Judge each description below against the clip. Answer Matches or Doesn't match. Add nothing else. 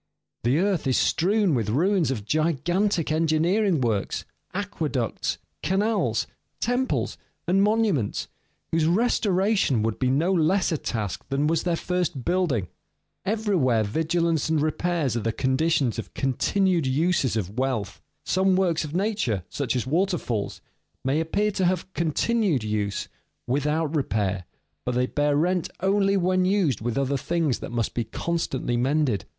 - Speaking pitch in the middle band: Matches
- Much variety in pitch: Matches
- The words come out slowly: Doesn't match